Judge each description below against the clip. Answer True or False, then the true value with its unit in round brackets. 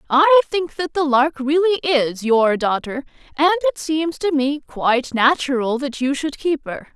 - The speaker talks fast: False (180 wpm)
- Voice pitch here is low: False (290 Hz)